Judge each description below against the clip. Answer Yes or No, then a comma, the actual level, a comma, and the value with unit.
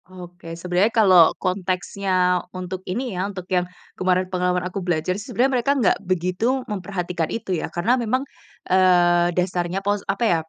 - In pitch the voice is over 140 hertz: Yes, medium, 185 Hz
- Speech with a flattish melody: Yes, narrow, 2.1 semitones